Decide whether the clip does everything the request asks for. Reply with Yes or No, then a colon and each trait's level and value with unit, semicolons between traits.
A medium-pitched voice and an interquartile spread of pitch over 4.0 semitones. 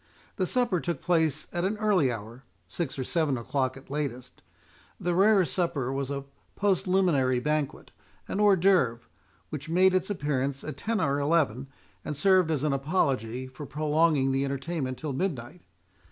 Yes: medium, 150 Hz; average, 5.0 semitones